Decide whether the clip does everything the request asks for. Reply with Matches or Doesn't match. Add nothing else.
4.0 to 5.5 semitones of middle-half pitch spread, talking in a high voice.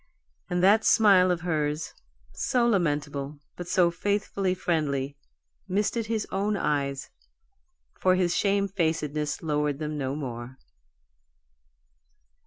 Doesn't match